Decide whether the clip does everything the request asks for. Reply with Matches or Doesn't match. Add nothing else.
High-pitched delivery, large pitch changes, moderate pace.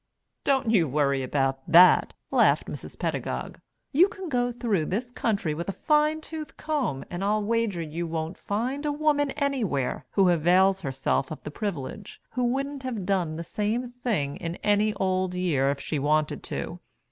Matches